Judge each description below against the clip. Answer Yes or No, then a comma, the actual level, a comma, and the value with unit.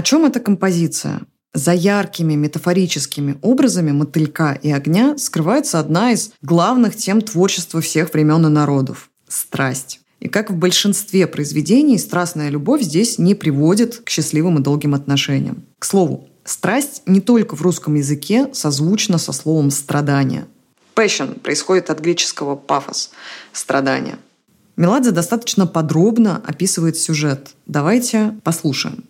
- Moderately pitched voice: Yes, medium, 170 Hz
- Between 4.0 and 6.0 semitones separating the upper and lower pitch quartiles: Yes, wide, 5.6 semitones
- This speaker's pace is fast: No, average, 130 wpm